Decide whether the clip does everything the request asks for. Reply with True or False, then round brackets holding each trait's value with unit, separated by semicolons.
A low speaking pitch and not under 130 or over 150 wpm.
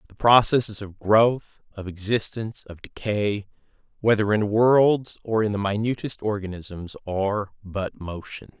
True (105 Hz; 135 wpm)